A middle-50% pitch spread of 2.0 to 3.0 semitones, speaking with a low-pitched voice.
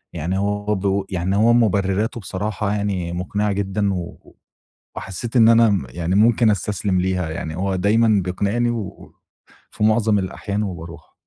Yes: narrow, 2.5 semitones; low, 100 Hz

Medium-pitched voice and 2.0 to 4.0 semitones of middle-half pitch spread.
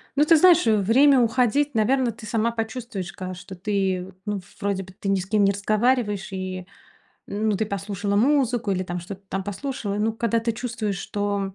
No: high, 210 Hz; average, 3.4 semitones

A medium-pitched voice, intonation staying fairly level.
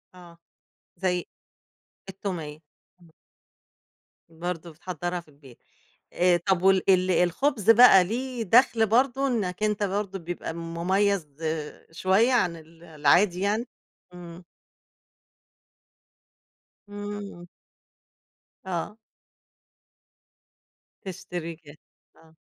No: medium, 180 Hz; average, 3.4 semitones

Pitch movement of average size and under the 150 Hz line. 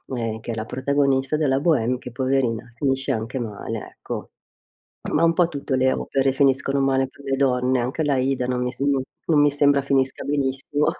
No: narrow, 1.9 semitones; low, 135 Hz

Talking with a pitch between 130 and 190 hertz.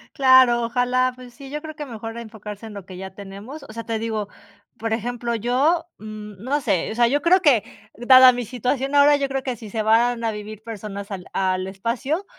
No: high, 235 Hz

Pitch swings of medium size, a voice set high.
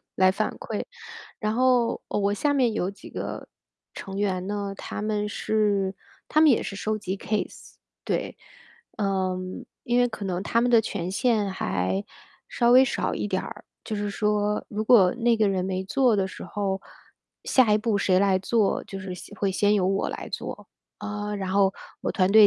No: narrow, 2.2 semitones; high, 205 Hz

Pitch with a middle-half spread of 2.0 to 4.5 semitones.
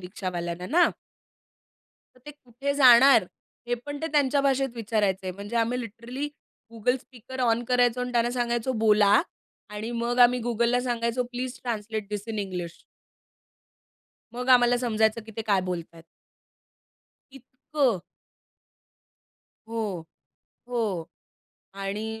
Yes: average, 3.1 semitones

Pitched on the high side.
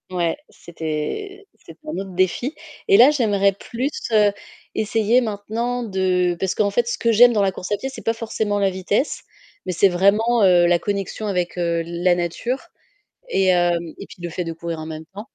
Yes: high, 200 Hz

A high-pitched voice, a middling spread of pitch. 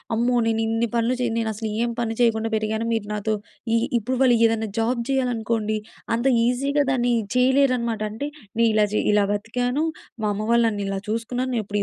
No: high, 230 Hz; narrow, 2.1 semitones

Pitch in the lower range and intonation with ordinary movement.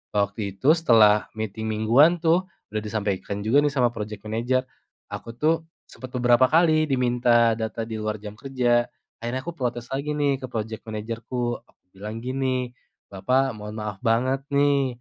Yes: low, 120 Hz; average, 3.6 semitones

